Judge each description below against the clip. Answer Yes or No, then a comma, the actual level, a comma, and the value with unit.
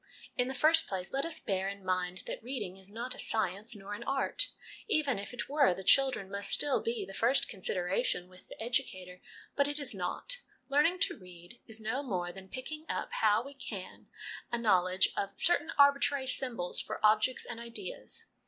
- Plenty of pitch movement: Yes, wide, 6.2 semitones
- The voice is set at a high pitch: Yes, high, 225 Hz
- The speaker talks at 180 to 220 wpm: Yes, average, 190 wpm